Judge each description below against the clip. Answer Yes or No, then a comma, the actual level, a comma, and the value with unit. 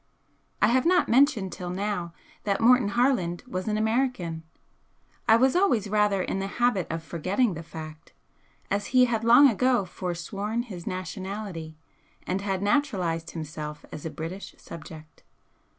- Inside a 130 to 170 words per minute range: Yes, average, 150 wpm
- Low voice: No, high, 195 Hz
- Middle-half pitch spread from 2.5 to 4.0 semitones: No, wide, 5.6 semitones